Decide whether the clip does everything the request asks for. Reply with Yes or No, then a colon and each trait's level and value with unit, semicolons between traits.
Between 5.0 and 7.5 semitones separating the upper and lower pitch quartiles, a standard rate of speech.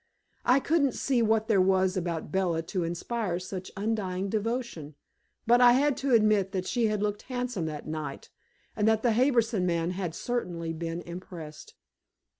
Yes: average, 5.3 semitones; average, 165 wpm